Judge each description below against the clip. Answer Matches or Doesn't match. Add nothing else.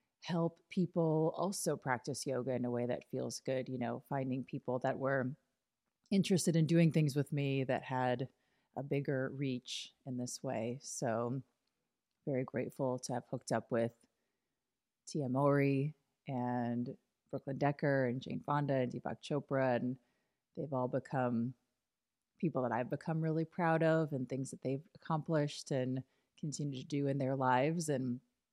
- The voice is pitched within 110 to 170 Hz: Matches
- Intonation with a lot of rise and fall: Doesn't match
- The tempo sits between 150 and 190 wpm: Matches